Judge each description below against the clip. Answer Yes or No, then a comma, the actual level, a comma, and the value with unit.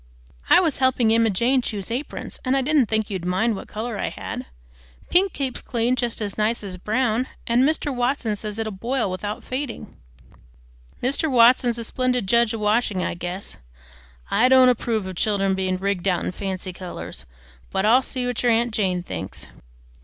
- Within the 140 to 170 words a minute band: No, average, 185 wpm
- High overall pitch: Yes, high, 225 Hz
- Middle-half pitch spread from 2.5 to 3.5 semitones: No, average, 4.1 semitones